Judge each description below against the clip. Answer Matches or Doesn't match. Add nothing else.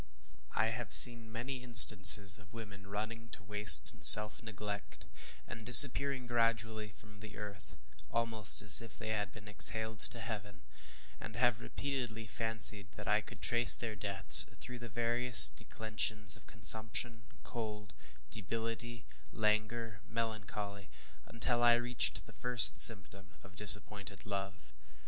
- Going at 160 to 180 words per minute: Doesn't match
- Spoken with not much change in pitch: Matches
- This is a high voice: Doesn't match